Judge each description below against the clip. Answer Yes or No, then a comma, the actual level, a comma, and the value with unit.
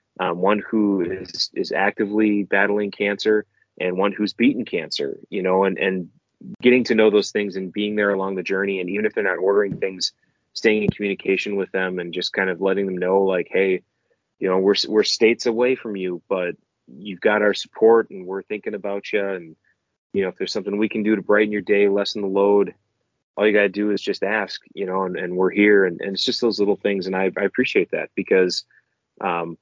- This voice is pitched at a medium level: No, low, 100 Hz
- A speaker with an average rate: No, fast, 225 wpm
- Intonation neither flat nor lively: No, narrow, 1.8 semitones